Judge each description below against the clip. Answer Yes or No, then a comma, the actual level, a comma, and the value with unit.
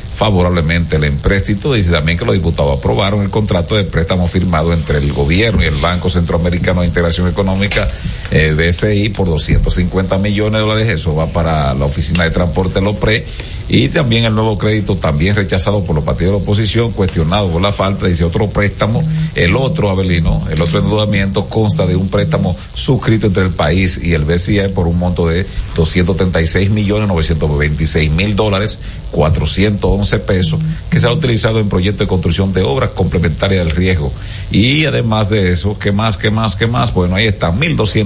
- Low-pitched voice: Yes, very low, 95 Hz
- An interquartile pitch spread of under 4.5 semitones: Yes, average, 3.8 semitones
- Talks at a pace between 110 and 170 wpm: No, average, 180 wpm